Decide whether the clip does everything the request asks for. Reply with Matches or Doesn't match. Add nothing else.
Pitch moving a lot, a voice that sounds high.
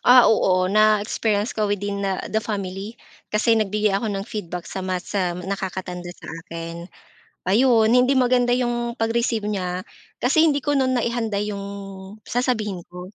Doesn't match